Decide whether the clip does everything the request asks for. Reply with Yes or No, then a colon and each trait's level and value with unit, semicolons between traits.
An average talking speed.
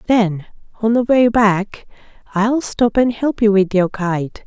Yes: average, 175 wpm